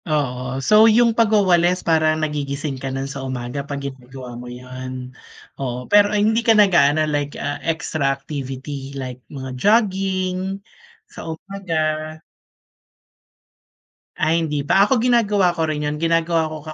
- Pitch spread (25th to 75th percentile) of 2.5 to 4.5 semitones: No, wide, 5.6 semitones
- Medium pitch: Yes, medium, 155 Hz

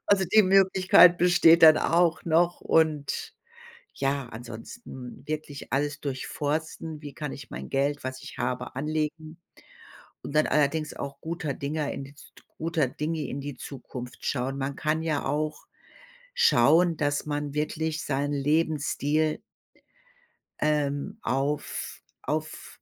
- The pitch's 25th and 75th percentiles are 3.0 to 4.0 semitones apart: No, narrow, 2.4 semitones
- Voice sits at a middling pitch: Yes, medium, 150 Hz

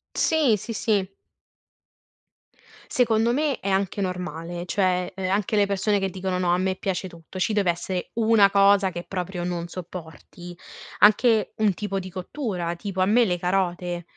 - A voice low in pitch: No, high, 190 Hz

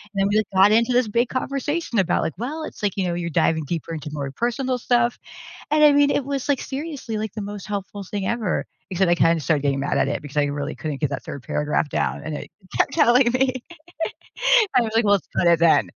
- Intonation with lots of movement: Yes, wide, 7.5 semitones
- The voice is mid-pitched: No, high, 205 Hz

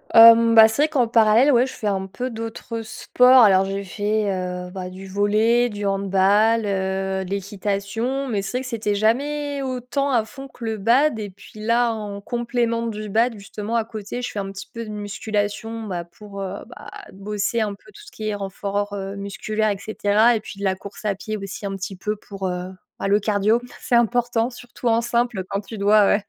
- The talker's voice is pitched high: Yes, high, 215 Hz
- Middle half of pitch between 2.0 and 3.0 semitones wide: Yes, average, 2.7 semitones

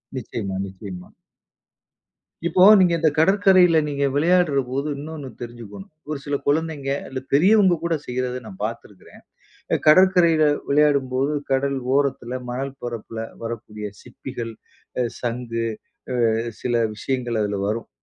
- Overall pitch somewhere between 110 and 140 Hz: Yes, low, 135 Hz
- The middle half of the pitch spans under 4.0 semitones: No, average, 4.8 semitones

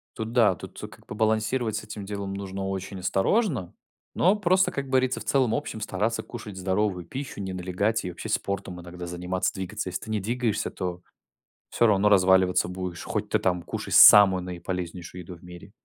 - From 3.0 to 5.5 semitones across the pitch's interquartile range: Yes, average, 3.3 semitones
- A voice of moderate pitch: No, very low, 95 Hz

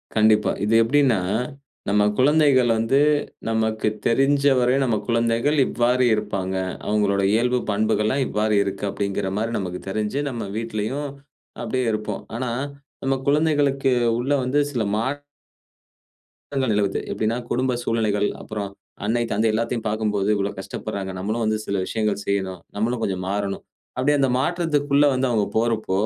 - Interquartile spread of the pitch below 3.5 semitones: No, average, 3.8 semitones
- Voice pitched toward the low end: Yes, low, 115 Hz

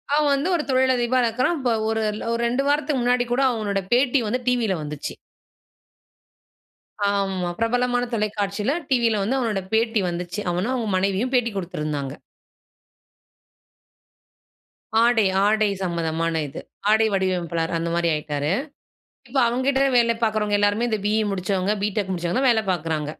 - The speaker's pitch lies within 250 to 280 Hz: No, high, 215 Hz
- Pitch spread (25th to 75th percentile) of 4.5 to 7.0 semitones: Yes, average, 5.0 semitones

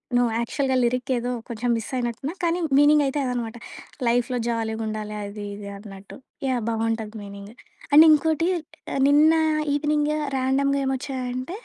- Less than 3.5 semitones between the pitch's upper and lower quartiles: No, average, 4.3 semitones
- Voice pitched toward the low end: No, high, 245 Hz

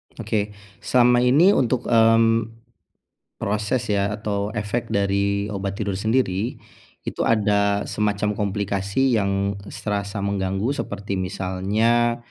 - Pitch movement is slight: Yes, narrow, 2.3 semitones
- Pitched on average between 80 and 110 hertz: Yes, low, 105 Hz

